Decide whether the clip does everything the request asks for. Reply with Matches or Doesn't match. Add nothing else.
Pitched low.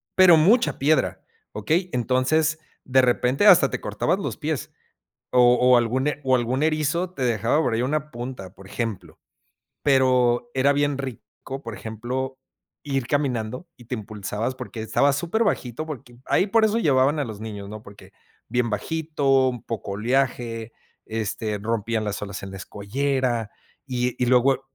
Matches